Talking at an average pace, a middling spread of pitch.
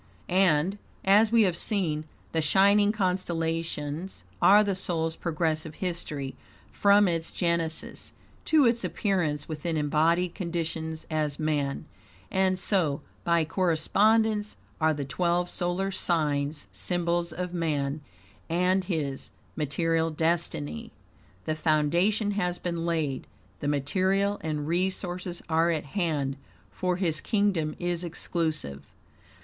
No: slow, 115 wpm; average, 3.3 semitones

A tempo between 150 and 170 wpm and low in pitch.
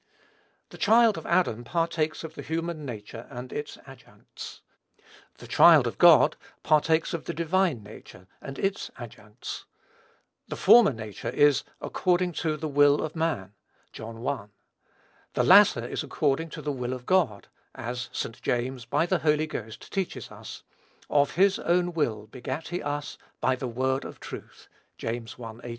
No: average, 160 wpm; medium, 145 Hz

